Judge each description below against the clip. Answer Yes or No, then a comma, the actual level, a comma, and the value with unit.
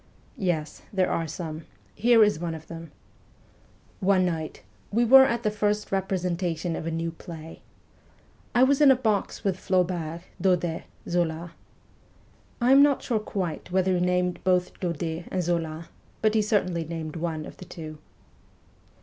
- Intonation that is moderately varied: Yes, average, 3.4 semitones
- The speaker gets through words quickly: No, average, 160 wpm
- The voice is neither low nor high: Yes, medium, 180 Hz